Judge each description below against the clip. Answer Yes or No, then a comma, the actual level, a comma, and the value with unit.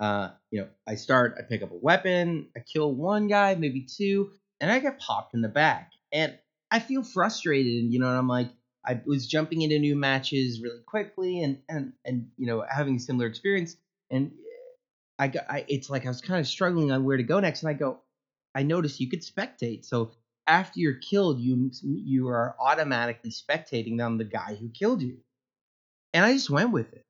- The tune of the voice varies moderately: No, wide, 6.7 semitones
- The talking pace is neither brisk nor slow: No, fast, 210 wpm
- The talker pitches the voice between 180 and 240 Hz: No, medium, 140 Hz